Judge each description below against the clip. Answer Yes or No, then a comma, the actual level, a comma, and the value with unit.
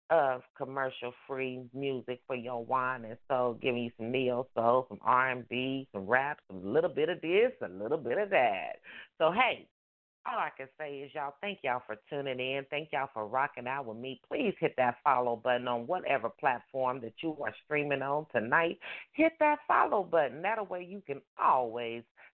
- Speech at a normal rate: Yes, average, 185 wpm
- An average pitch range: Yes, average, 3.8 semitones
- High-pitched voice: No, low, 130 Hz